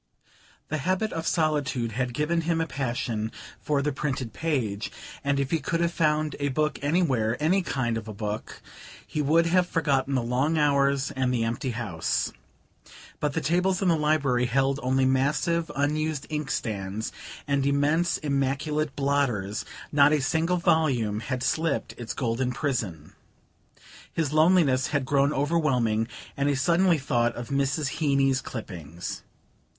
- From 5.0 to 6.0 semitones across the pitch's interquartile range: No, average, 3.8 semitones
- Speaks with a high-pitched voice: No, medium, 140 Hz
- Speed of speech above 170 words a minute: No, average, 150 wpm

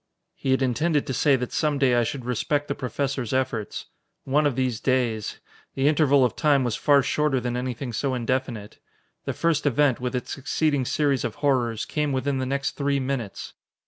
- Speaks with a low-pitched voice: Yes, low, 130 Hz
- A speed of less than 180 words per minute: No, average, 190 wpm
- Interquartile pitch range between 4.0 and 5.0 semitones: No, narrow, 2.5 semitones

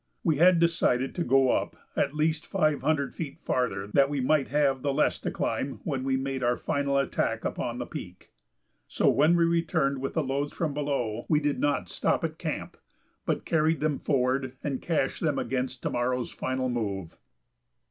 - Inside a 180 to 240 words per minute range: Yes, average, 190 wpm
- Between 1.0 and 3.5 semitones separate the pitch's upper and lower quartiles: Yes, average, 2.9 semitones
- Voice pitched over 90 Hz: Yes, medium, 140 Hz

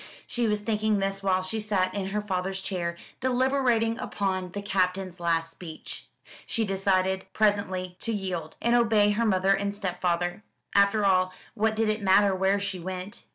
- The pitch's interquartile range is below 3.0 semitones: Yes, narrow, 2.4 semitones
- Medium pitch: No, high, 195 Hz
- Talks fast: No, average, 165 wpm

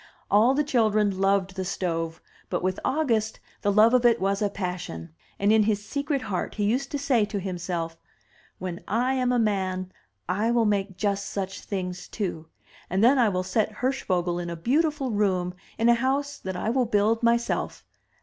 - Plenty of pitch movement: No, average, 4.2 semitones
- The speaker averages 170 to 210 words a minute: Yes, average, 190 wpm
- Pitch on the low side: No, high, 205 Hz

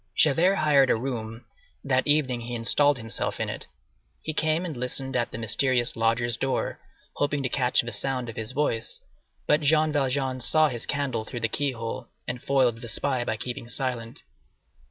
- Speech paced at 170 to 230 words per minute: Yes, average, 180 wpm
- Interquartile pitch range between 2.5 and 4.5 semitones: Yes, average, 3.4 semitones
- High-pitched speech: No, low, 130 Hz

